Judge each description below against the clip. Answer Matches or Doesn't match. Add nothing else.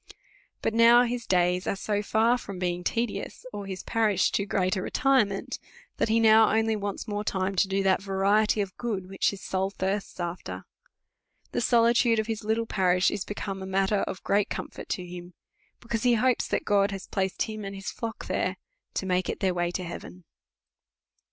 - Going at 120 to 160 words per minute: Doesn't match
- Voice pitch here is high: Matches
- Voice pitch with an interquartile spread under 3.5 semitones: Matches